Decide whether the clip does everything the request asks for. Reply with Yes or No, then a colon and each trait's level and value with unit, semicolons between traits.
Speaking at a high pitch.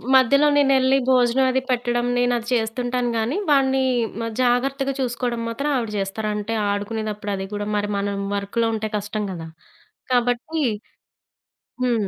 Yes: high, 240 Hz